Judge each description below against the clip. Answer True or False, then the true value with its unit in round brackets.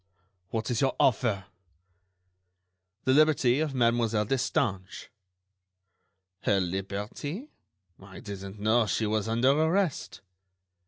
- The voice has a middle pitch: False (115 Hz)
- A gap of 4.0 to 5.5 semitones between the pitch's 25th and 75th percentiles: True (5.0 semitones)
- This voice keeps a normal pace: False (100 wpm)